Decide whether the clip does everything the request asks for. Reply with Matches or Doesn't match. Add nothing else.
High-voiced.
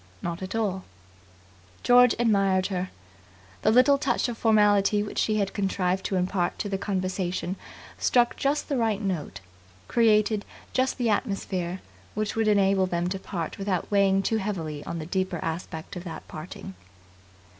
Matches